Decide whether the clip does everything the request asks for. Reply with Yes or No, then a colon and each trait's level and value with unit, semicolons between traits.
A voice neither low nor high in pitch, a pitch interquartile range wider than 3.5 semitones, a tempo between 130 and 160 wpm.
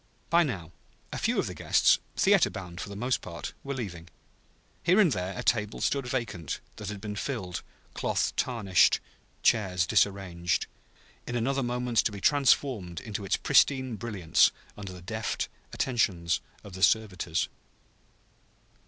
No: low, 105 Hz; average, 5.2 semitones; average, 150 wpm